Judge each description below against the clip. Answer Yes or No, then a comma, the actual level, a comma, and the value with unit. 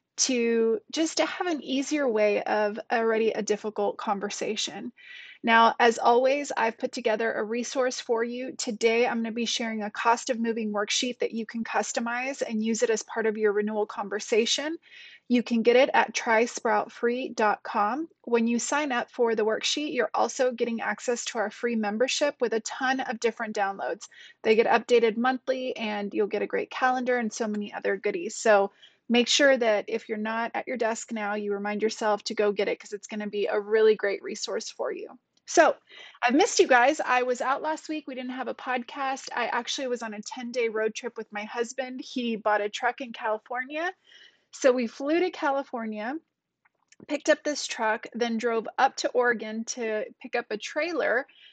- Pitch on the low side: No, high, 235 Hz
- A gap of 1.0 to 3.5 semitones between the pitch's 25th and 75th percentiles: Yes, average, 3.1 semitones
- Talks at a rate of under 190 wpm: No, average, 195 wpm